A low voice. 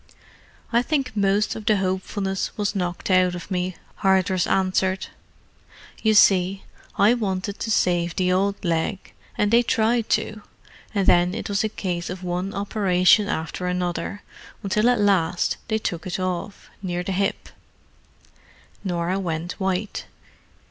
No: high, 190 Hz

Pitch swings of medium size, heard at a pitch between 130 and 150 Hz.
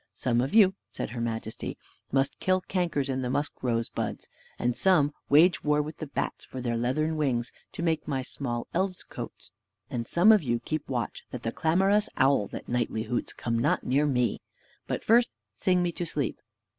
No: wide, 5.9 semitones; medium, 140 Hz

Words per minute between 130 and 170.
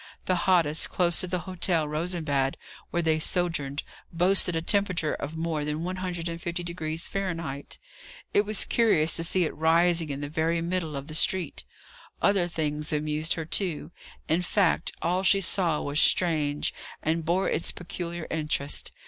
Yes: average, 155 wpm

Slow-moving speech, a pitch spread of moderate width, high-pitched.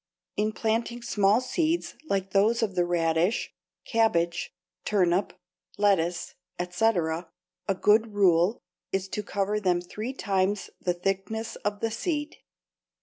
Yes: slow, 125 wpm; average, 3.9 semitones; high, 200 Hz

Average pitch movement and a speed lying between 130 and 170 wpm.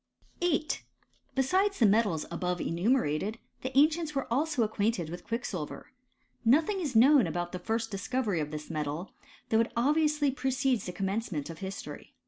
No: wide, 7.3 semitones; average, 155 wpm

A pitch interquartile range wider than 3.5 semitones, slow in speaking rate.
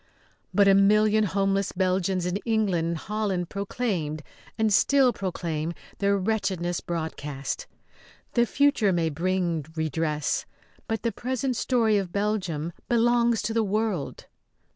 Yes: average, 4.3 semitones; slow, 125 wpm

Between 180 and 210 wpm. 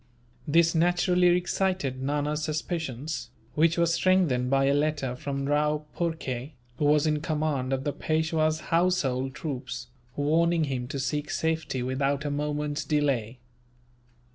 No: slow, 135 wpm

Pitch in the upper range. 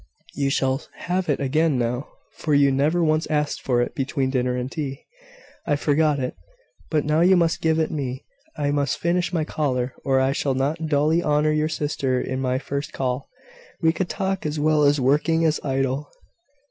No: medium, 145 Hz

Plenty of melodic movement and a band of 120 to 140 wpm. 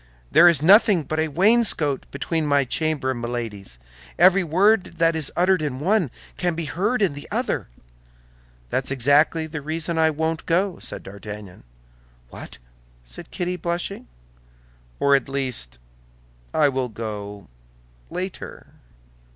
Yes: wide, 6.0 semitones; slow, 135 wpm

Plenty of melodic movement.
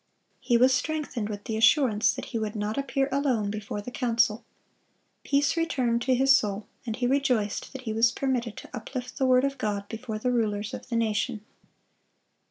No: average, 3.5 semitones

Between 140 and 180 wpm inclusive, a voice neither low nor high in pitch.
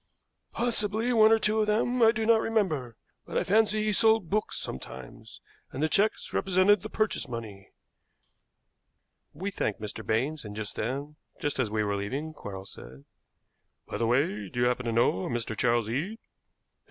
Yes: average, 175 wpm; medium, 145 Hz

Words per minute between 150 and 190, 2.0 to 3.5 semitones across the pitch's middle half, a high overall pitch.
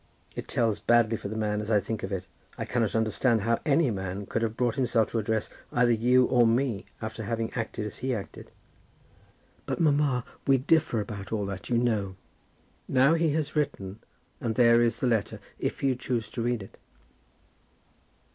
No: average, 185 wpm; average, 2.8 semitones; low, 115 Hz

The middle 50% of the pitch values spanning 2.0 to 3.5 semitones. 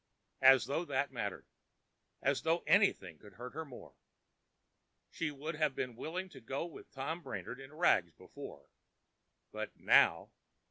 No: average, 4.3 semitones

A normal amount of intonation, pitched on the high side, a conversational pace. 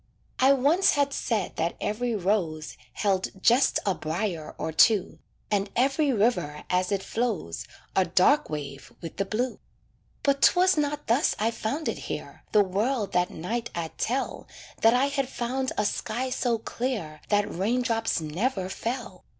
No: wide, 5.7 semitones; high, 220 Hz; average, 160 wpm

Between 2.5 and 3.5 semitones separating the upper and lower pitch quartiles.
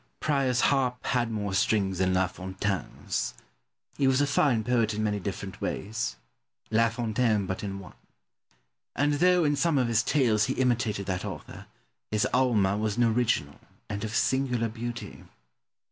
No: average, 3.9 semitones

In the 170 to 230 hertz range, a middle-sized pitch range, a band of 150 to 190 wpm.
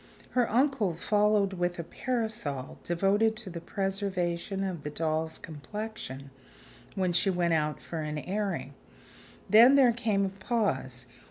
No: high, 190 Hz; average, 4.6 semitones; average, 140 wpm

